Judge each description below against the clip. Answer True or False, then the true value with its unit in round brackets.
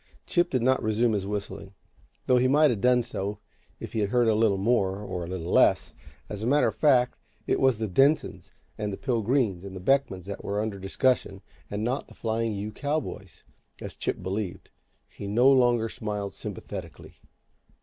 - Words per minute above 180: True (190 wpm)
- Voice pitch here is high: False (110 Hz)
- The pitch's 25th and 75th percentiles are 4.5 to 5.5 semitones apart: False (4.1 semitones)